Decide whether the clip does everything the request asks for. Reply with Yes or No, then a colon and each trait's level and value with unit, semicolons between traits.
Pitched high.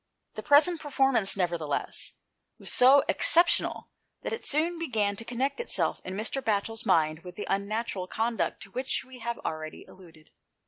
Yes: high, 225 Hz